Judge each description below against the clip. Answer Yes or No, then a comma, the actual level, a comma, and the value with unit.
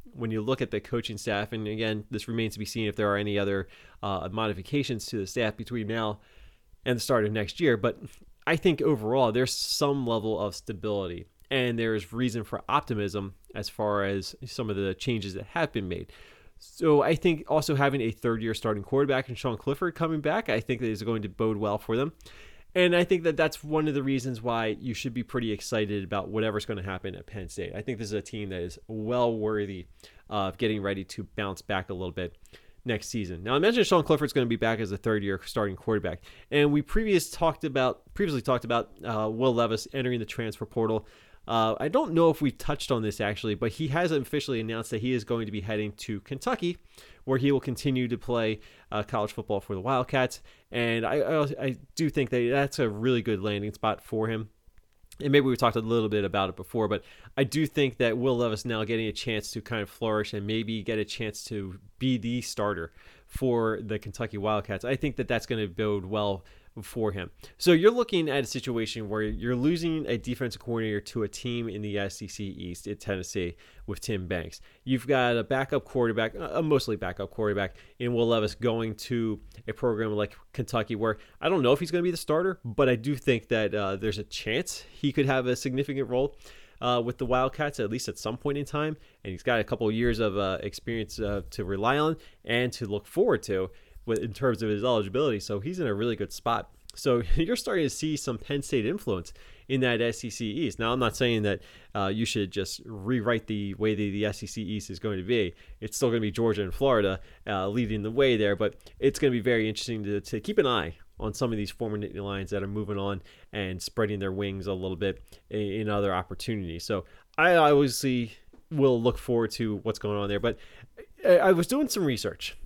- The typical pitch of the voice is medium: No, low, 110 Hz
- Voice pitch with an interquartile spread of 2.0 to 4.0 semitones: Yes, average, 3.7 semitones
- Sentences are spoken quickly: Yes, fast, 225 wpm